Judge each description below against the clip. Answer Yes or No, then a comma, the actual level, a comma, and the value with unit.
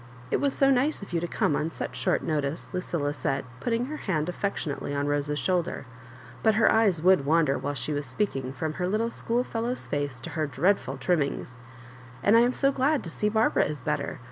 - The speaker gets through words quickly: Yes, fast, 215 wpm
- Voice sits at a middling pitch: Yes, medium, 165 Hz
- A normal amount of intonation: No, wide, 7.5 semitones